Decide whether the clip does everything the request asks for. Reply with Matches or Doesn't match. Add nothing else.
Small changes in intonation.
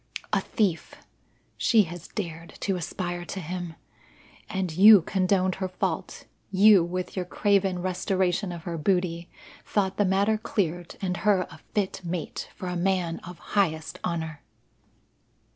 Matches